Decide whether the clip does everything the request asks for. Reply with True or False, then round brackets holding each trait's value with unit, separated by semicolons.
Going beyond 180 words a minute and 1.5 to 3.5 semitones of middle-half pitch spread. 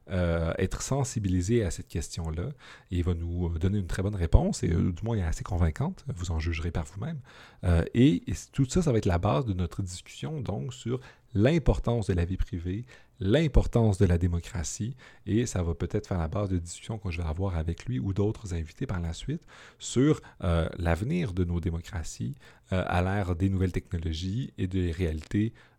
False (200 wpm; 4.9 semitones)